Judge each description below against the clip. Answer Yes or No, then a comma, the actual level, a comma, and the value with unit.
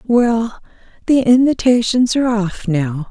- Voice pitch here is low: No, high, 225 Hz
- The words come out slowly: Yes, slow, 115 wpm